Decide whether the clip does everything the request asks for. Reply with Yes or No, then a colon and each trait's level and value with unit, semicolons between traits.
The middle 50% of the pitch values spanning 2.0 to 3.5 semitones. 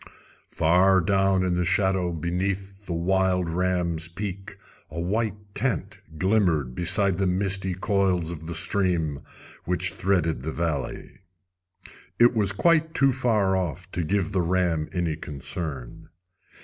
Yes: average, 2.7 semitones